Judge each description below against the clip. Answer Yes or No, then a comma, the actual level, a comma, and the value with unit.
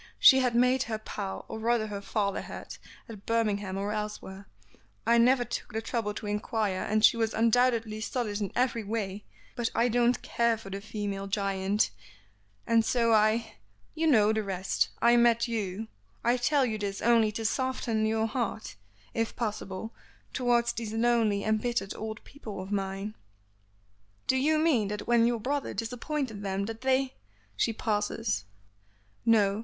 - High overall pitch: Yes, high, 220 Hz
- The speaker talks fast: No, average, 165 wpm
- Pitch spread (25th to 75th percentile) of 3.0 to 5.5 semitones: No, narrow, 2.5 semitones